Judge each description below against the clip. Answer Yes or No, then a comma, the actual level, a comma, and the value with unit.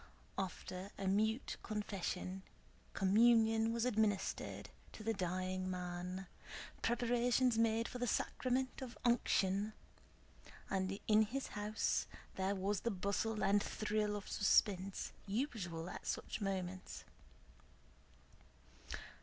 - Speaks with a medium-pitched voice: No, high, 205 Hz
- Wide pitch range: No, average, 3.1 semitones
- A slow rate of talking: Yes, slow, 105 wpm